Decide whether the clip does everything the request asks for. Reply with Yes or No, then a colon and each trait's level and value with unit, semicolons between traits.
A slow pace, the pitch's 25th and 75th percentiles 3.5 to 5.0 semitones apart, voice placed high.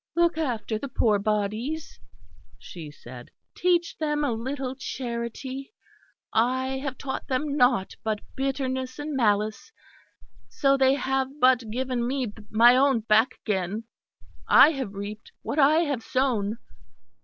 Yes: slow, 130 wpm; average, 3.9 semitones; very high, 255 Hz